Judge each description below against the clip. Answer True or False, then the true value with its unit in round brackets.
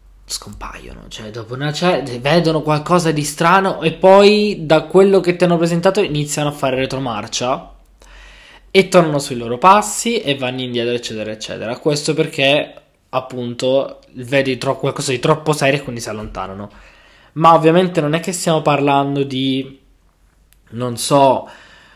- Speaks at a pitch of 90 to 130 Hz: False (140 Hz)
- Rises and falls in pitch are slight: False (4.7 semitones)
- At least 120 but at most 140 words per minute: False (150 wpm)